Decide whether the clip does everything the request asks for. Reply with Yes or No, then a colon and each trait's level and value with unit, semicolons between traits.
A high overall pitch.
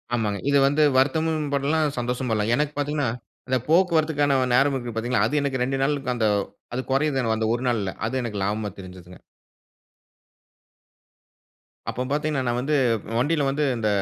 No: low, 135 Hz